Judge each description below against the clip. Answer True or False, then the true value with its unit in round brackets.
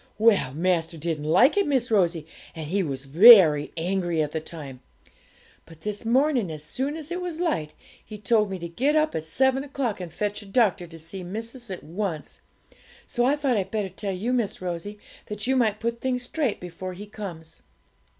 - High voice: True (200 Hz)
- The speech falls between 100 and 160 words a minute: False (200 wpm)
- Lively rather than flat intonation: True (6.4 semitones)